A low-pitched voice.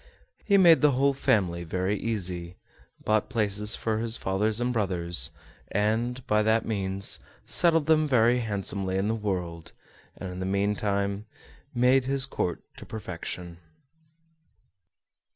Yes: low, 105 Hz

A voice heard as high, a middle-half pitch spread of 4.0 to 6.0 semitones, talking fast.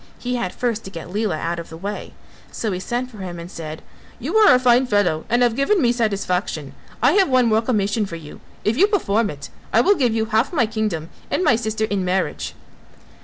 Yes: high, 220 Hz; average, 5.1 semitones; fast, 225 wpm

